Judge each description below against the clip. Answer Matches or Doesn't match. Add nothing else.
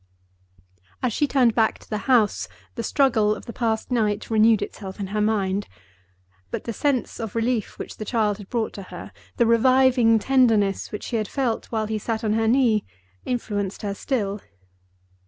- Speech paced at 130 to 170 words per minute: Doesn't match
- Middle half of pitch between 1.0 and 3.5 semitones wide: Matches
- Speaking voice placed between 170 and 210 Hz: Doesn't match